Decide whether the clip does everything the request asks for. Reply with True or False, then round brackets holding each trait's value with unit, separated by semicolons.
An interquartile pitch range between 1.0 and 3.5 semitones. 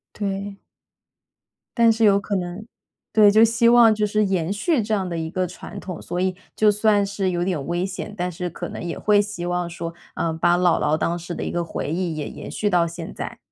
True (3.2 semitones)